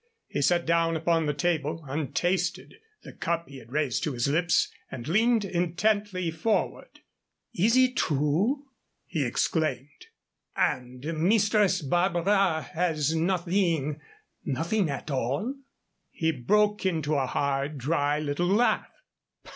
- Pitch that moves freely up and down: No, average, 4.4 semitones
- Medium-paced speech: No, slow, 125 wpm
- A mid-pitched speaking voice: Yes, medium, 165 Hz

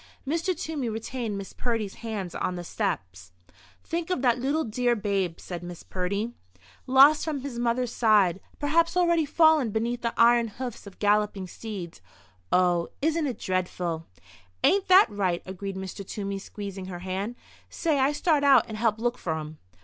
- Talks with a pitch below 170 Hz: No, high, 220 Hz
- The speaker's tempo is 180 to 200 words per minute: No, average, 160 wpm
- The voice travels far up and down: Yes, wide, 6.1 semitones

